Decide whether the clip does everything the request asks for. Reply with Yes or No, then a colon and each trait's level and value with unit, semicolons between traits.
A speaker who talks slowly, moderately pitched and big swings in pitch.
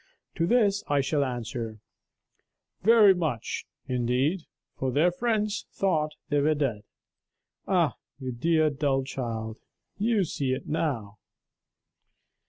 Yes: slow, 115 wpm; medium, 145 Hz; wide, 6.1 semitones